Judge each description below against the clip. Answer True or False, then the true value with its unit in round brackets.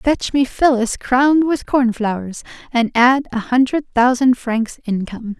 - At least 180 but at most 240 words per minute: False (155 wpm)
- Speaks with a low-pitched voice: False (250 Hz)